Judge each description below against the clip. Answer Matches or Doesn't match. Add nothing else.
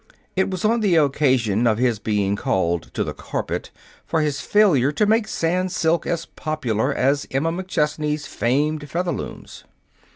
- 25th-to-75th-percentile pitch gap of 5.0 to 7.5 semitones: Matches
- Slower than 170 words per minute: Matches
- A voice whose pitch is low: Doesn't match